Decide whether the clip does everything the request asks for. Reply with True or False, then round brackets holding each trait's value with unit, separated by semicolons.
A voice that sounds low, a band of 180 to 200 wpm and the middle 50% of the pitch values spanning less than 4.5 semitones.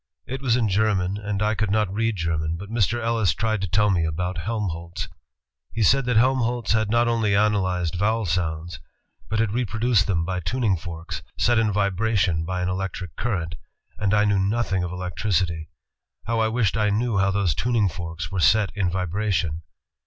True (100 Hz; 185 wpm; 3.7 semitones)